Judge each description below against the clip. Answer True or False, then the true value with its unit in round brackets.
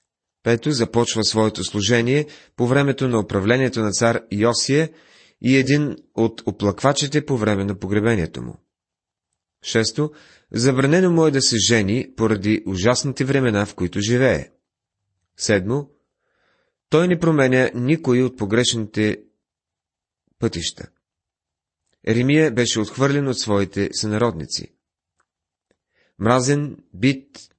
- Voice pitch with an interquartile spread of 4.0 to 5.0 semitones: True (4.6 semitones)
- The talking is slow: True (105 wpm)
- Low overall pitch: True (120 Hz)